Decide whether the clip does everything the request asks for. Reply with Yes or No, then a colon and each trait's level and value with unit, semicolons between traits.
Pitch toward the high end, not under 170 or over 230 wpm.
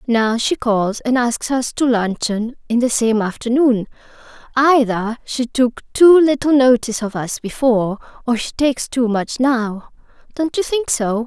No: high, 245 Hz; average, 160 wpm